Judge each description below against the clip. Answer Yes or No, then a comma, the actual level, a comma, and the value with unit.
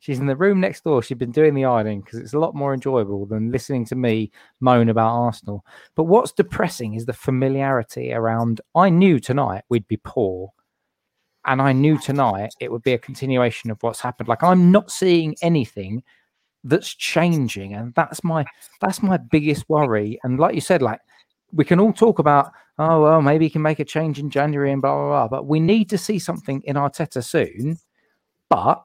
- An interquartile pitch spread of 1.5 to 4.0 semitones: No, average, 5.3 semitones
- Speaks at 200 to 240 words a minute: Yes, fast, 205 wpm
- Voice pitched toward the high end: No, low, 135 Hz